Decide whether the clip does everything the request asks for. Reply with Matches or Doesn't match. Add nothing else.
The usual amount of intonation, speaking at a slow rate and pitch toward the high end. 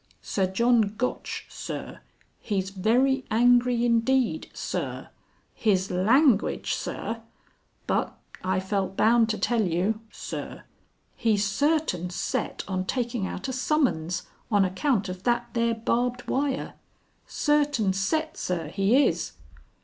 Matches